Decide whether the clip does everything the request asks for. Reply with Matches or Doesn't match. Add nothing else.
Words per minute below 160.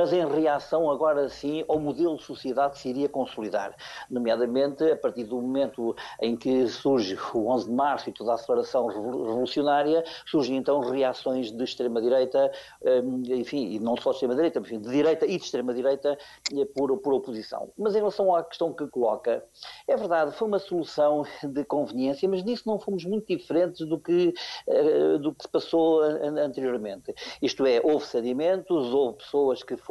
Doesn't match